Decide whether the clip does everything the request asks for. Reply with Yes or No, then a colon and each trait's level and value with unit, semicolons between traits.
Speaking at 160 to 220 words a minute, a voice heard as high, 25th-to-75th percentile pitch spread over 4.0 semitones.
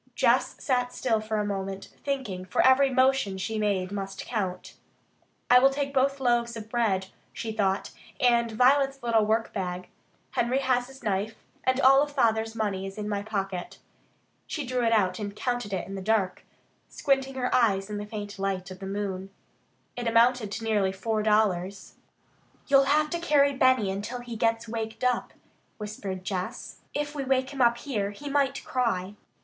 Yes: average, 175 wpm; high, 225 Hz; average, 4.6 semitones